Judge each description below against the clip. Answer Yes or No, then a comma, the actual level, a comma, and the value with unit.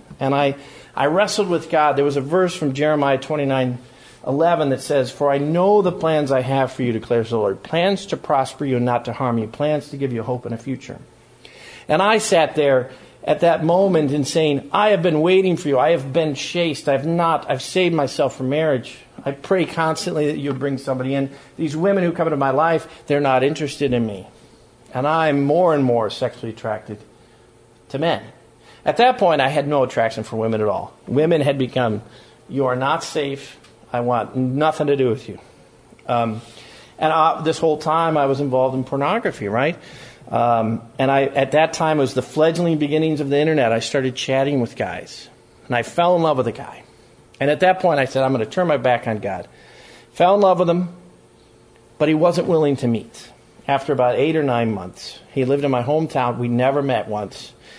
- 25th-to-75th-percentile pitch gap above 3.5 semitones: Yes, average, 4.5 semitones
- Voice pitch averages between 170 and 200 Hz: No, medium, 140 Hz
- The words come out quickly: Yes, fast, 210 wpm